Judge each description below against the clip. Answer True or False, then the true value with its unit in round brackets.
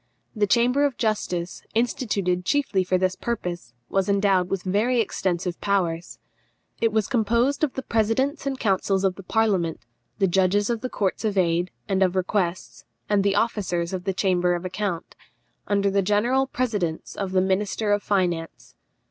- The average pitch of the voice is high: True (195 Hz)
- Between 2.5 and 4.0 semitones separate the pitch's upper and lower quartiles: True (3.4 semitones)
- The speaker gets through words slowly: False (165 wpm)